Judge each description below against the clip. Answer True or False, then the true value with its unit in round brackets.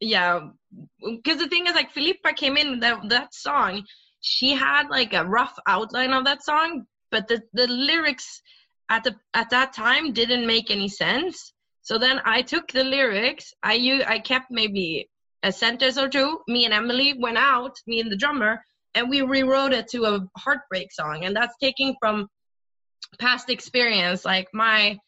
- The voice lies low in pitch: False (245 Hz)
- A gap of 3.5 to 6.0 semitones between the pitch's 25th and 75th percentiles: True (3.9 semitones)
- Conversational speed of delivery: True (175 wpm)